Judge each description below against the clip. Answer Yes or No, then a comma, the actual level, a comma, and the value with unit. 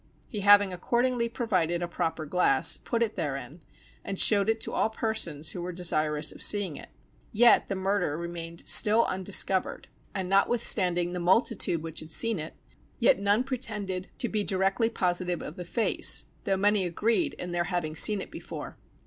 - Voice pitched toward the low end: No, high, 190 Hz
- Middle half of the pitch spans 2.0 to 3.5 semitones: No, average, 4.0 semitones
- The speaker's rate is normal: Yes, average, 175 wpm